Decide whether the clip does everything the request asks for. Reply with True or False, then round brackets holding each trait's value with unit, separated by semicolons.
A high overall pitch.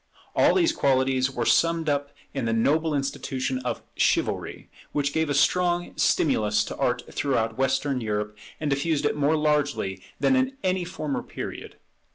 False (140 Hz)